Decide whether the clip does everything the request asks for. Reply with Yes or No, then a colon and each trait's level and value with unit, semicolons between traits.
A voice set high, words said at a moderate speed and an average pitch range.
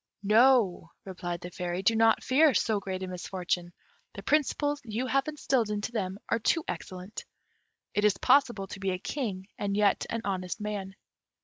Yes: high, 205 Hz; average, 175 wpm; average, 4.2 semitones